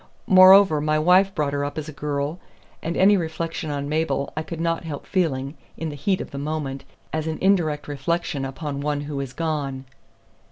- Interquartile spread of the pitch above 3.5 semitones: No, average, 2.7 semitones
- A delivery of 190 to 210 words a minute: Yes, average, 195 wpm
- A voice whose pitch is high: No, medium, 155 Hz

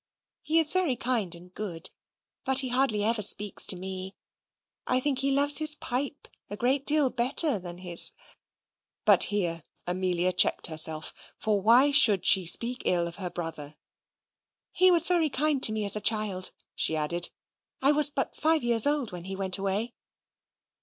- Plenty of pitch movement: Yes, wide, 7.1 semitones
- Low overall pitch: No, high, 215 Hz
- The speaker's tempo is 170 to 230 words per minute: Yes, average, 175 wpm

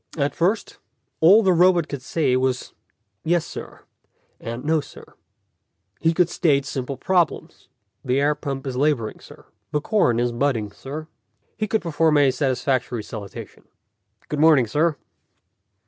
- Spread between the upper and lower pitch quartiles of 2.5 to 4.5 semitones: Yes, average, 4.1 semitones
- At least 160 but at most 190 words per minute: No, average, 145 wpm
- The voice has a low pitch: No, medium, 145 Hz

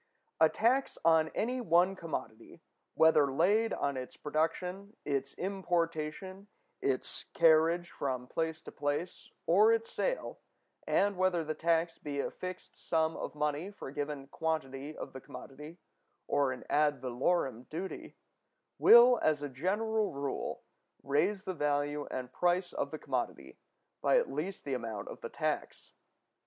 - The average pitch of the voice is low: No, medium, 160 Hz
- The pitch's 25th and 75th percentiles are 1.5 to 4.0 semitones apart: No, average, 4.6 semitones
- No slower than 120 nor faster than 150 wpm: Yes, average, 145 wpm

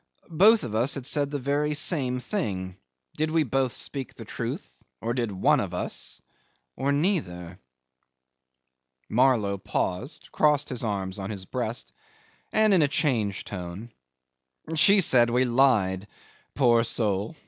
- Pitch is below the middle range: Yes, low, 120 Hz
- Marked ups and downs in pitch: Yes, wide, 6.5 semitones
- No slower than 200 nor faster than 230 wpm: No, average, 145 wpm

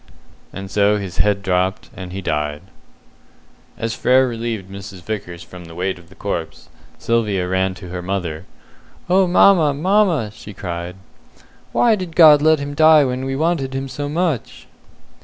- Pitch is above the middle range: No, low, 105 Hz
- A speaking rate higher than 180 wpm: No, average, 160 wpm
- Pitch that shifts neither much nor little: No, wide, 7.7 semitones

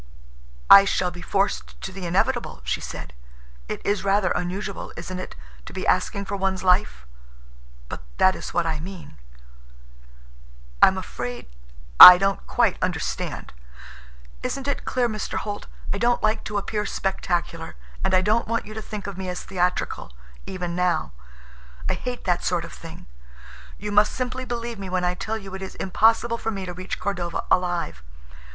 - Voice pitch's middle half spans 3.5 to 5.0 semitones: No, average, 2.8 semitones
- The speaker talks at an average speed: Yes, average, 165 wpm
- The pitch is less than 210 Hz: Yes, high, 190 Hz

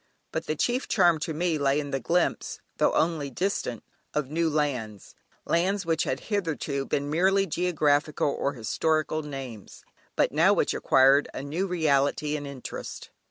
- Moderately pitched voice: Yes, medium, 150 Hz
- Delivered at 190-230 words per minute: No, average, 160 wpm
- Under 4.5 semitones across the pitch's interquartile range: Yes, average, 3.3 semitones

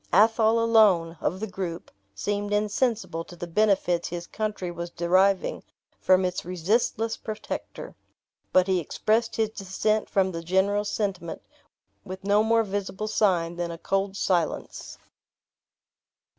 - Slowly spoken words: Yes, slow, 130 wpm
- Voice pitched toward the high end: Yes, high, 195 Hz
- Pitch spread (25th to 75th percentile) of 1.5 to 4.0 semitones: Yes, average, 3.5 semitones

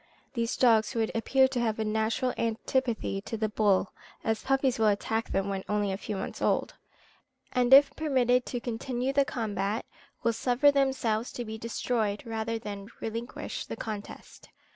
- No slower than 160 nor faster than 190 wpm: Yes, average, 165 wpm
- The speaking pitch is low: No, high, 225 Hz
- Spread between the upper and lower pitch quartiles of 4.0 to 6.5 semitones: No, narrow, 2.6 semitones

